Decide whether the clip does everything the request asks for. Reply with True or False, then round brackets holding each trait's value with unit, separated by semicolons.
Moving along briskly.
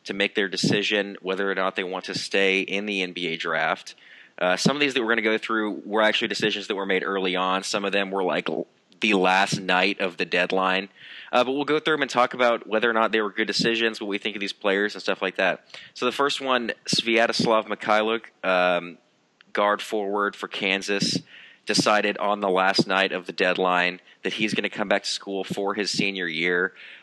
True (220 wpm)